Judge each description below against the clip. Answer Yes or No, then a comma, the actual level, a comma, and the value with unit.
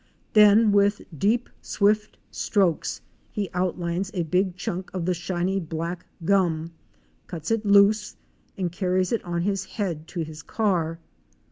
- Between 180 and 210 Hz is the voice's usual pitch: Yes, medium, 185 Hz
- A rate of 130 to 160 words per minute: Yes, average, 140 wpm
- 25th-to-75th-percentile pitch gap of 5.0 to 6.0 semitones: No, average, 3.0 semitones